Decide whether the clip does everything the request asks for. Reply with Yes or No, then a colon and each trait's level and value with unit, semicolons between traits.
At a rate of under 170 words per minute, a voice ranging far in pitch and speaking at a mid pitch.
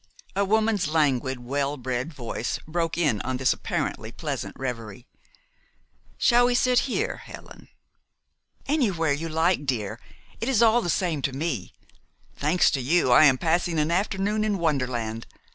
Yes: average, 150 wpm; wide, 7.0 semitones; medium, 155 Hz